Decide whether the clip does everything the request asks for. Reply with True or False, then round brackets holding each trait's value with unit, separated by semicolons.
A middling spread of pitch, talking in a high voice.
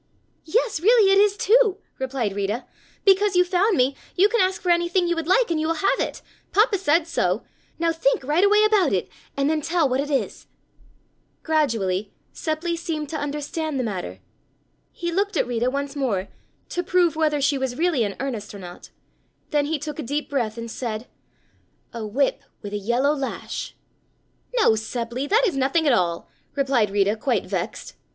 False (6.1 semitones; 295 Hz)